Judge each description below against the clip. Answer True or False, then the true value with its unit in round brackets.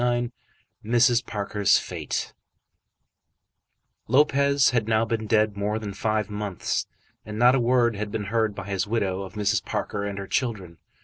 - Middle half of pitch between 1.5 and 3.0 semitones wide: True (2.7 semitones)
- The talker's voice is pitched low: True (110 Hz)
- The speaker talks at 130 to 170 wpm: True (165 wpm)